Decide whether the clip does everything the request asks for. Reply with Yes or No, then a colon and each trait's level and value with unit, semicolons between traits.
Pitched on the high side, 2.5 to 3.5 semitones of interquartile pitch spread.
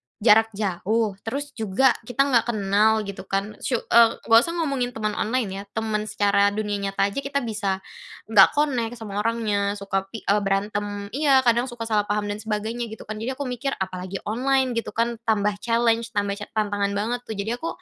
Yes: high, 220 Hz; average, 2.8 semitones